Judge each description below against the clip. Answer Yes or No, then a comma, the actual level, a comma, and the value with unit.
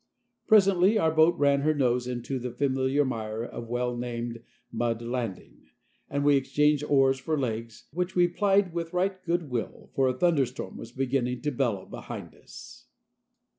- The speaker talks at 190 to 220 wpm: No, average, 165 wpm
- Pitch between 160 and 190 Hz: No, low, 135 Hz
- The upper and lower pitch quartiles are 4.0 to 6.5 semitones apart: Yes, average, 4.8 semitones